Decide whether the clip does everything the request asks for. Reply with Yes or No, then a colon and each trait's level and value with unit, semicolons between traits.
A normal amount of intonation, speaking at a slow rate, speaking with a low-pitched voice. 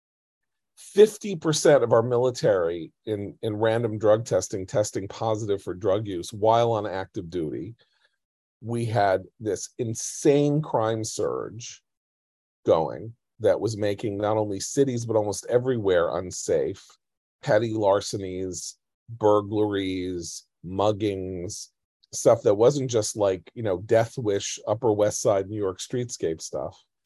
Yes: average, 3.1 semitones; slow, 120 wpm; low, 110 Hz